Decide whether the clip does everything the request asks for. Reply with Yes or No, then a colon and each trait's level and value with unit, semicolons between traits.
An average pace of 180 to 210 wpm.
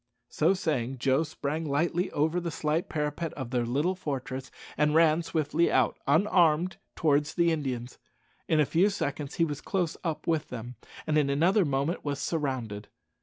No: average, 170 wpm